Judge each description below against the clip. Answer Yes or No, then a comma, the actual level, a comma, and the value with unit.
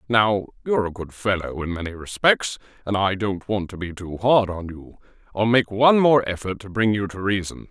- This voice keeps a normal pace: No, fast, 220 wpm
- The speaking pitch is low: Yes, low, 100 Hz